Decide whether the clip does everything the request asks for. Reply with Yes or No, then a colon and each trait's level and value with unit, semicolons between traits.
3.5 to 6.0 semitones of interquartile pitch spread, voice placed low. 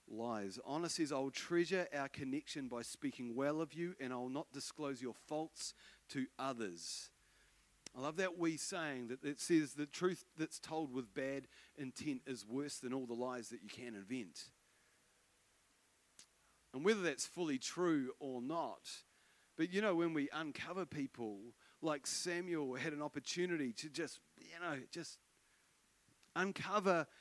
No: average, 4.6 semitones; medium, 145 Hz